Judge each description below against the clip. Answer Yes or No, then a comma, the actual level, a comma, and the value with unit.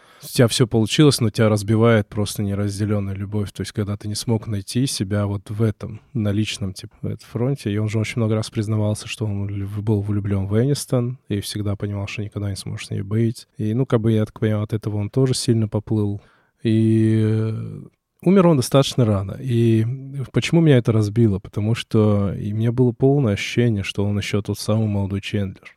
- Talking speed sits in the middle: No, fast, 205 wpm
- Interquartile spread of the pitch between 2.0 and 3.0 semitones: Yes, narrow, 2.6 semitones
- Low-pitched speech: Yes, low, 110 Hz